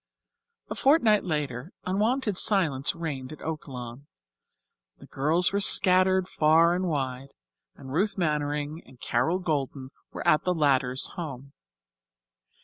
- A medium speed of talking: No, slow, 125 wpm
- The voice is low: No, medium, 155 Hz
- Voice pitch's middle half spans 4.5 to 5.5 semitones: Yes, average, 5.1 semitones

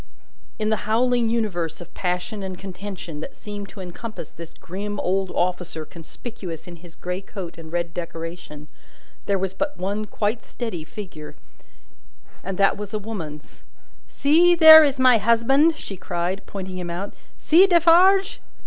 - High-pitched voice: Yes, high, 195 Hz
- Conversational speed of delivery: Yes, average, 155 wpm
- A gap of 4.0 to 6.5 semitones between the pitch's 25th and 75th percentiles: Yes, average, 4.7 semitones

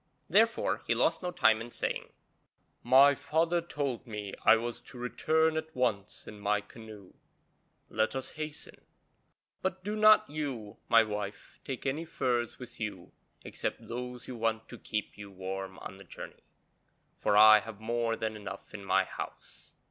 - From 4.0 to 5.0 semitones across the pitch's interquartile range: Yes, average, 4.6 semitones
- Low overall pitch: Yes, low, 115 Hz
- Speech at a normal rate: Yes, average, 165 wpm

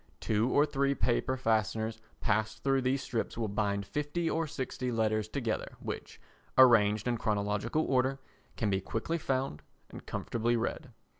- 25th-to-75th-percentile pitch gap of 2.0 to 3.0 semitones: No, average, 3.7 semitones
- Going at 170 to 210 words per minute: No, average, 150 wpm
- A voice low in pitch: Yes, low, 115 Hz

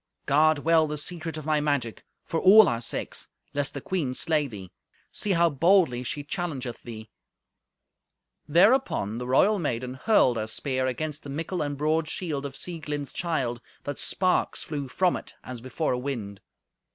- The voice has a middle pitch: Yes, medium, 145 Hz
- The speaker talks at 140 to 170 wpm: Yes, average, 165 wpm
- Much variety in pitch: No, average, 4.4 semitones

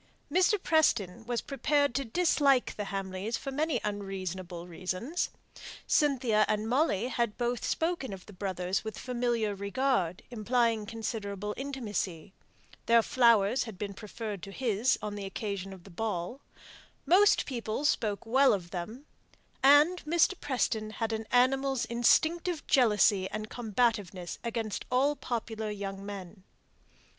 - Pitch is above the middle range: Yes, high, 225 Hz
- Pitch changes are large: No, average, 4.6 semitones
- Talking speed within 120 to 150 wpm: Yes, slow, 135 wpm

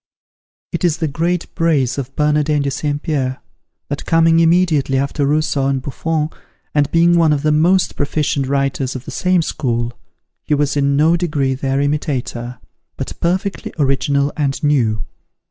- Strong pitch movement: No, average, 3.0 semitones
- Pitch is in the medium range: Yes, medium, 145 Hz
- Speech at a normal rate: Yes, average, 160 wpm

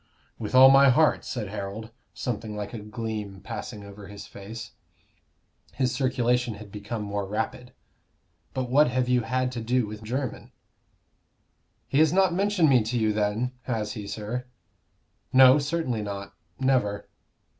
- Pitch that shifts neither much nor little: Yes, average, 3.5 semitones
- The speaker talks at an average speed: Yes, average, 150 wpm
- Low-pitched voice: Yes, low, 115 Hz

